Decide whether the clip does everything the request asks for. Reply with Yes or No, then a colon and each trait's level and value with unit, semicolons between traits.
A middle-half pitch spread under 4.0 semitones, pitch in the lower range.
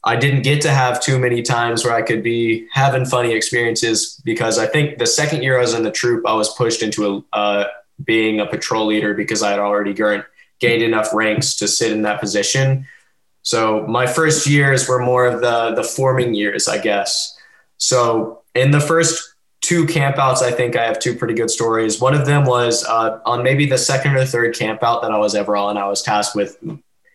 Yes: average, 3.6 semitones; low, 120 Hz